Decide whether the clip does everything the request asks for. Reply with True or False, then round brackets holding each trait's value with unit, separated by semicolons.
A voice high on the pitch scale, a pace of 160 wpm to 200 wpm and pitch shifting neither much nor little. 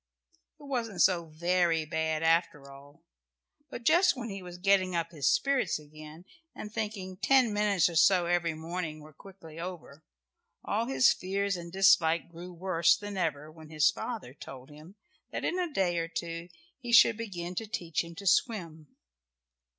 False (175 Hz; 170 wpm; 3.8 semitones)